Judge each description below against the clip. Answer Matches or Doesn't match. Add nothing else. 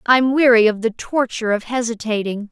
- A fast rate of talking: Doesn't match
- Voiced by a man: Doesn't match